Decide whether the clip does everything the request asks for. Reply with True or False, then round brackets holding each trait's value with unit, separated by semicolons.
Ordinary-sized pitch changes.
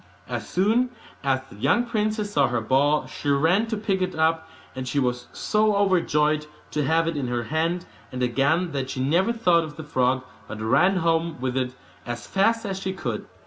False (6.5 semitones)